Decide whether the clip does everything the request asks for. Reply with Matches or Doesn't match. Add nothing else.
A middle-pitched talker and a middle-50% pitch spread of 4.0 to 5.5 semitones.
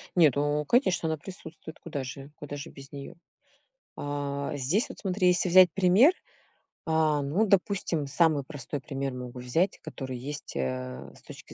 Matches